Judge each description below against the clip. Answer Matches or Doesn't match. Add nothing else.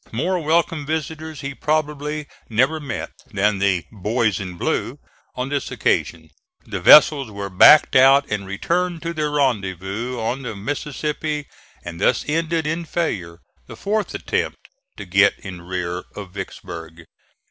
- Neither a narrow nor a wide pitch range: Doesn't match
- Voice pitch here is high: Doesn't match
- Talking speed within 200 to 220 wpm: Doesn't match